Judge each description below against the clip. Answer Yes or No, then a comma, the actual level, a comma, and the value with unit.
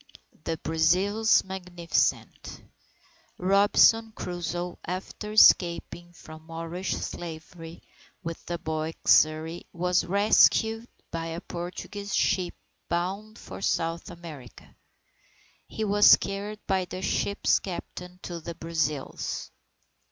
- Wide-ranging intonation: No, average, 3.1 semitones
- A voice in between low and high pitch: Yes, medium, 175 Hz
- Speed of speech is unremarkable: No, slow, 100 wpm